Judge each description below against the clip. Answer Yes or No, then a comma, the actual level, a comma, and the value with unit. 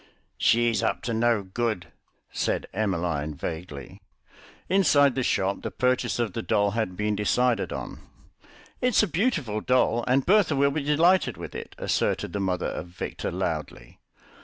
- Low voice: Yes, low, 115 Hz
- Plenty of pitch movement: Yes, wide, 6.3 semitones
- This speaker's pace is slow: No, average, 155 wpm